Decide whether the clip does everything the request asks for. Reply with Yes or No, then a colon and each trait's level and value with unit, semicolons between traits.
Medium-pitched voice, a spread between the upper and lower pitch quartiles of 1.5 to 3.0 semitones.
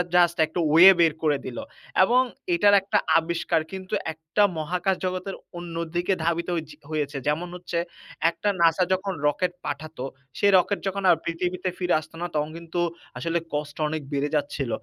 Yes: medium, 170 Hz; average, 2.7 semitones